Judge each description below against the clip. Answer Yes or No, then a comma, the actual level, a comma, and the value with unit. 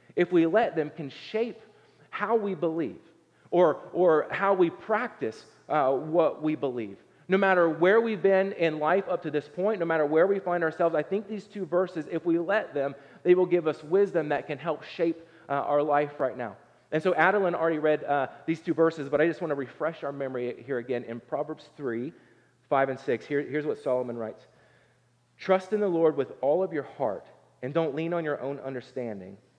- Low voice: No, medium, 160 Hz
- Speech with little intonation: No, average, 4.2 semitones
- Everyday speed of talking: No, fast, 210 wpm